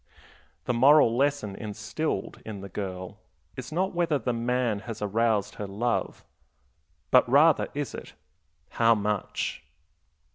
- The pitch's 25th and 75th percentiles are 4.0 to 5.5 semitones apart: Yes, average, 4.6 semitones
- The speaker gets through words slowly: Yes, slow, 130 wpm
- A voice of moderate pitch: No, low, 115 Hz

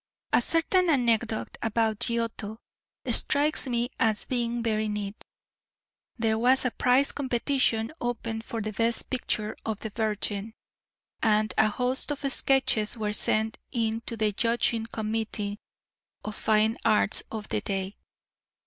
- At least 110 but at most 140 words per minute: Yes, slow, 135 wpm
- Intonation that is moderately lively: No, narrow, 2.1 semitones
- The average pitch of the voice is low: No, high, 225 Hz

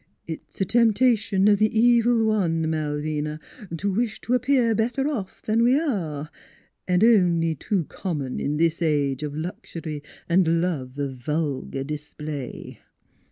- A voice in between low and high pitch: Yes, medium, 170 Hz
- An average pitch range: No, wide, 6.6 semitones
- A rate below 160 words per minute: Yes, average, 150 wpm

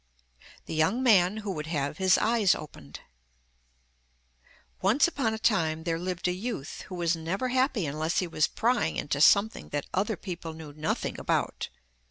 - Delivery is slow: No, average, 165 wpm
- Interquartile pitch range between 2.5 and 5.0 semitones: No, wide, 5.5 semitones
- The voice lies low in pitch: No, medium, 180 Hz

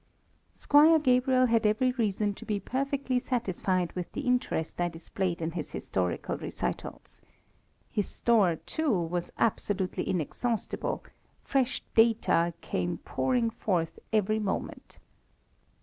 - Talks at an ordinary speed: No, slow, 120 wpm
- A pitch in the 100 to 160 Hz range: No, high, 215 Hz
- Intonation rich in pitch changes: Yes, wide, 6.1 semitones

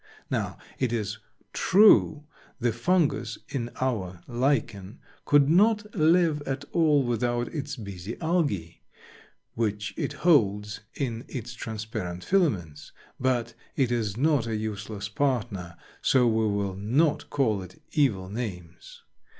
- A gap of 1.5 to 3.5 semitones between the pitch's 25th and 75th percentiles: No, wide, 5.6 semitones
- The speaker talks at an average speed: No, slow, 125 wpm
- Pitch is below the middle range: Yes, low, 120 Hz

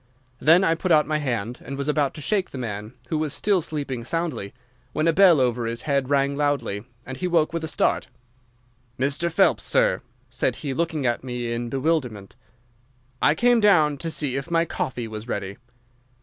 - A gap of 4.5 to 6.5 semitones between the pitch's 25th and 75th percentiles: Yes, average, 5.1 semitones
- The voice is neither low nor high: Yes, medium, 145 Hz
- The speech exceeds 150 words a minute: Yes, average, 190 wpm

